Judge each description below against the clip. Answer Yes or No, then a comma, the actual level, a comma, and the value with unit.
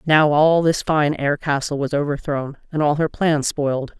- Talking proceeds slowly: No, average, 195 wpm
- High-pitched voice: No, medium, 150 Hz